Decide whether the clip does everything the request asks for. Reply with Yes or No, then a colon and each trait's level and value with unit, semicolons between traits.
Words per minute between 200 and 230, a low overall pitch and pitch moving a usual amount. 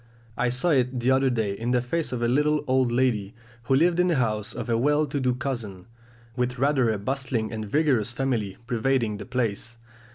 Yes: fast, 205 wpm; low, 125 Hz; average, 3.0 semitones